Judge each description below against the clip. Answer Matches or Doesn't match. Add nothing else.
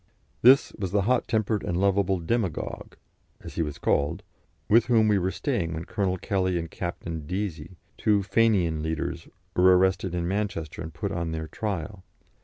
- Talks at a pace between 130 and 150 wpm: Doesn't match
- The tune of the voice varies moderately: Matches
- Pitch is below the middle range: Matches